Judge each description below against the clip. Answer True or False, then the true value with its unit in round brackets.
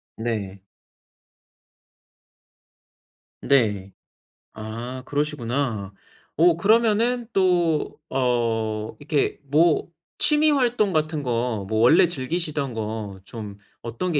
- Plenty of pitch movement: True (7.3 semitones)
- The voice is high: False (135 Hz)